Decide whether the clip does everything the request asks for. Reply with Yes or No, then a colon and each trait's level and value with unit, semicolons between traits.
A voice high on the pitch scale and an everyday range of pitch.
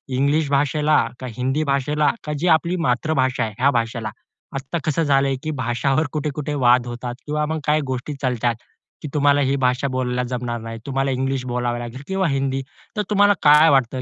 No: low, 135 Hz; average, 3.3 semitones